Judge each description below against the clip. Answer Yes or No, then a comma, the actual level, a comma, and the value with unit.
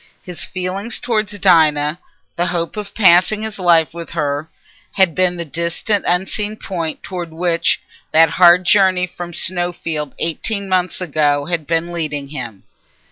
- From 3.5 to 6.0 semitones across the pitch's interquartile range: No, narrow, 2.5 semitones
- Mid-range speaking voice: Yes, medium, 175 Hz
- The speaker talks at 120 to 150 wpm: Yes, average, 145 wpm